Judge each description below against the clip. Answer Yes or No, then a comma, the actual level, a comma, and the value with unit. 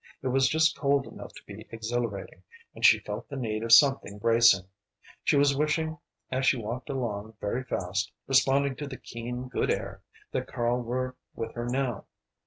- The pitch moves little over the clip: No, average, 3.2 semitones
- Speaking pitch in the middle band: No, low, 125 Hz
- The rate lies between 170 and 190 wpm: Yes, average, 180 wpm